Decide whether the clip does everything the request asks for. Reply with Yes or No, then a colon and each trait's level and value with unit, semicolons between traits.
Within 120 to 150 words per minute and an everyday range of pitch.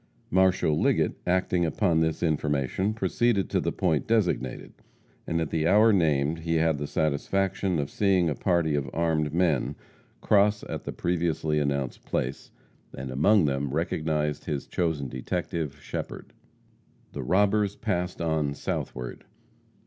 Yes: average, 140 wpm; average, 4.1 semitones